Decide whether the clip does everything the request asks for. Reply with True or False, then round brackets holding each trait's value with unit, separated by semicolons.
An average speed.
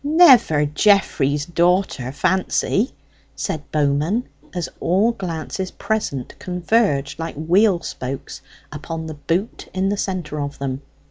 False (120 wpm)